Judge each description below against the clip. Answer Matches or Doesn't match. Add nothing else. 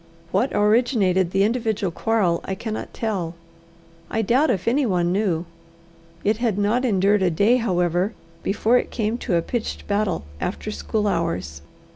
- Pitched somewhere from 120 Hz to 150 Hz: Doesn't match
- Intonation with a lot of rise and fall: Doesn't match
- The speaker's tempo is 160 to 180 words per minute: Doesn't match